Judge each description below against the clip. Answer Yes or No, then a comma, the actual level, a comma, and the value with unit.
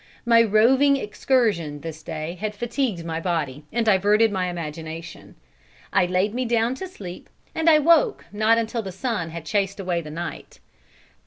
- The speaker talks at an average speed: Yes, average, 165 wpm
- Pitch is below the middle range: No, high, 205 Hz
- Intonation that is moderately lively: No, wide, 5.7 semitones